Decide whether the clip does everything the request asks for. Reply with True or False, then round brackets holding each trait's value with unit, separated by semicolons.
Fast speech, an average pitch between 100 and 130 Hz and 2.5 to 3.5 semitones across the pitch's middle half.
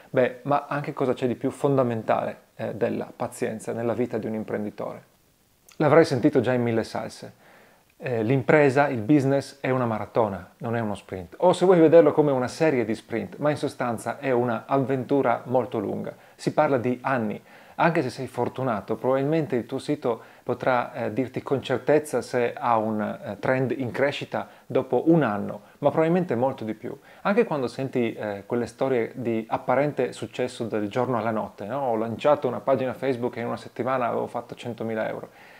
True (180 wpm; 125 Hz; 3.1 semitones)